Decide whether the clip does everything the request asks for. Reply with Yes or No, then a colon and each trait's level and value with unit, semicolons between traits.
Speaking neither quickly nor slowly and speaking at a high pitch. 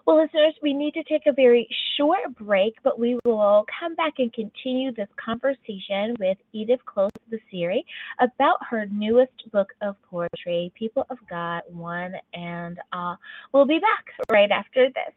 Yes: average, 165 wpm; high, 235 Hz